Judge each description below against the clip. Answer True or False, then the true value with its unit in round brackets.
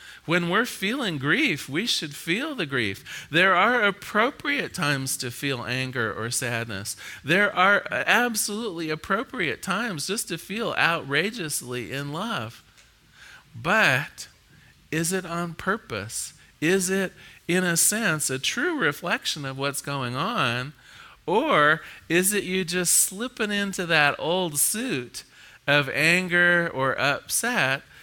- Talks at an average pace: False (130 wpm)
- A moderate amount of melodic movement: False (5.8 semitones)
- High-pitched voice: False (170 Hz)